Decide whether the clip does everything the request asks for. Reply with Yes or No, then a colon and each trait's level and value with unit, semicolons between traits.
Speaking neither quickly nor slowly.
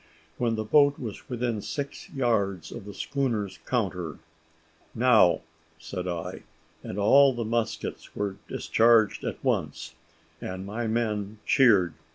No: slow, 130 wpm